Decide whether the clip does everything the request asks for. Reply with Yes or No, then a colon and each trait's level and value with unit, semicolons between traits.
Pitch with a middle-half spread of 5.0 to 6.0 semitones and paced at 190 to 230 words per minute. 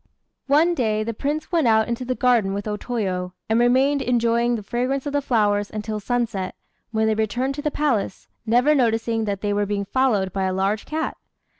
No: average, 3.8 semitones; average, 200 wpm